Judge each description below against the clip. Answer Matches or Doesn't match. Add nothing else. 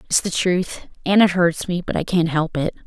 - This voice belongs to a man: Doesn't match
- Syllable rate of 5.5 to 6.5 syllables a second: Doesn't match